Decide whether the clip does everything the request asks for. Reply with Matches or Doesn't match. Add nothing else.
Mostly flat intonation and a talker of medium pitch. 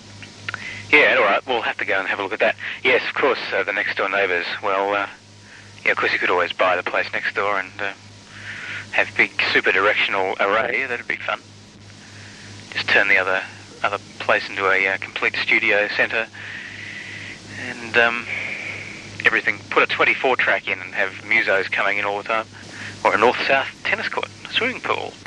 Doesn't match